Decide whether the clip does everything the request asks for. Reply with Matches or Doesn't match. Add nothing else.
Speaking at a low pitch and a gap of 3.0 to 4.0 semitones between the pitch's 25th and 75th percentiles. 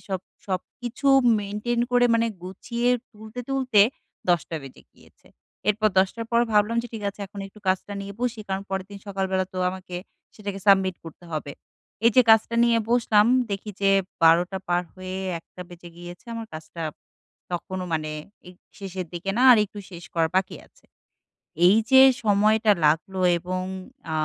Doesn't match